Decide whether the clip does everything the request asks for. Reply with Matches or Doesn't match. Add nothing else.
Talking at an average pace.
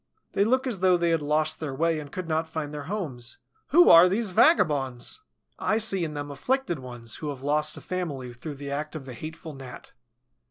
Doesn't match